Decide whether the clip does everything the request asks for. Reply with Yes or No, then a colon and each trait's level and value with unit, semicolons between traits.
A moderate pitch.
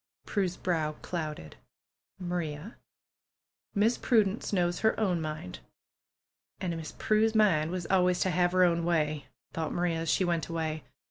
Yes: medium, 175 Hz